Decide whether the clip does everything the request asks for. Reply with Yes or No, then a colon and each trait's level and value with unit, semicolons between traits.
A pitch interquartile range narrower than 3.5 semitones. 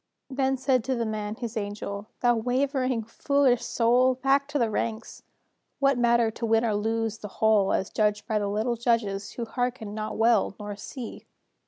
Yes: average, 2.9 semitones